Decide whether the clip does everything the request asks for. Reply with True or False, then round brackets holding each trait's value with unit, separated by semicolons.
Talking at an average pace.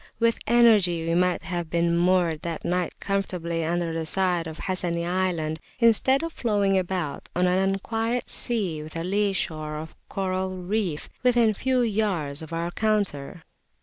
True (165 wpm)